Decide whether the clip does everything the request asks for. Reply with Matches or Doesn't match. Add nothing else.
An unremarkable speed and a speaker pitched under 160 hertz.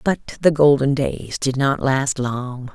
Matches